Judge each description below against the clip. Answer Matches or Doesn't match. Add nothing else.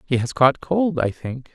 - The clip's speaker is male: Matches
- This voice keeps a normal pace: Doesn't match